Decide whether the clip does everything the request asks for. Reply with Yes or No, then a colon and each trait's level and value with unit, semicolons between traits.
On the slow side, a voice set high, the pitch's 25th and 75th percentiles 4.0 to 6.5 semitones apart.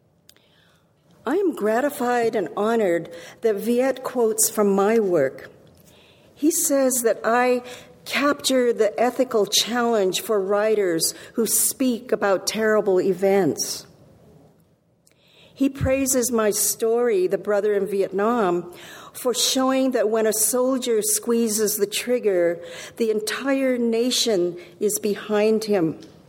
No: slow, 110 wpm; high, 220 Hz; average, 3.3 semitones